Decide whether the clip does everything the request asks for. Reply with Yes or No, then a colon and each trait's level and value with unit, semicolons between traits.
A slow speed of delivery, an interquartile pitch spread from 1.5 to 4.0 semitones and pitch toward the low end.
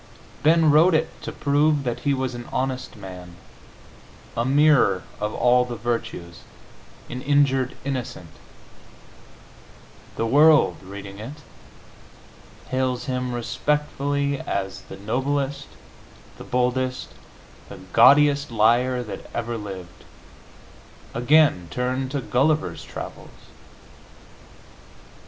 Yes: slow, 100 wpm; average, 3.6 semitones; low, 130 Hz